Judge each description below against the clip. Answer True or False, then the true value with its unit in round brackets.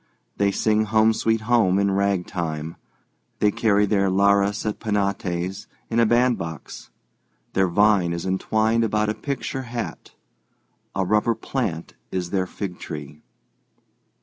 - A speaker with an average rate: False (130 wpm)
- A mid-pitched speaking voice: False (100 Hz)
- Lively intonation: False (2.8 semitones)